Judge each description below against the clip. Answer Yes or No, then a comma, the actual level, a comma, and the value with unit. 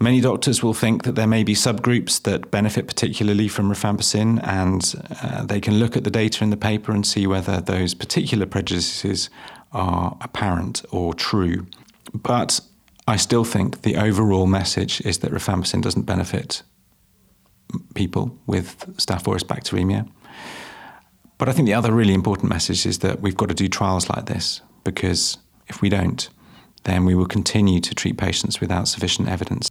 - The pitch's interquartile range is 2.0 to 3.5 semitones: Yes, narrow, 2.6 semitones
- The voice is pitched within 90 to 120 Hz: Yes, low, 100 Hz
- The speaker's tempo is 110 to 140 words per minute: No, average, 165 wpm